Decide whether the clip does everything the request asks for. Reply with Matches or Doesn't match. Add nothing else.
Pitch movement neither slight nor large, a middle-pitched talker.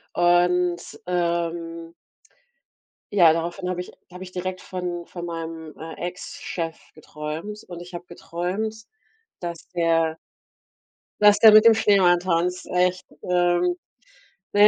Doesn't match